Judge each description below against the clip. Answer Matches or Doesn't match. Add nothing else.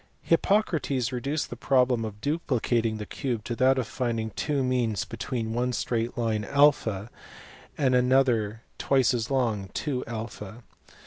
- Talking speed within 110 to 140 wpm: Matches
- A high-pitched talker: Doesn't match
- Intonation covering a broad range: Doesn't match